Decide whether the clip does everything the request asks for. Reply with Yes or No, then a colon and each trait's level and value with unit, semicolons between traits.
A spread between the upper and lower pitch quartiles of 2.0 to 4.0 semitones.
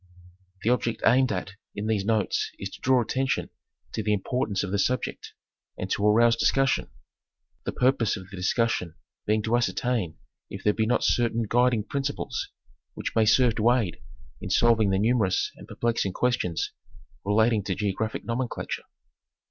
Yes: average, 3.2 semitones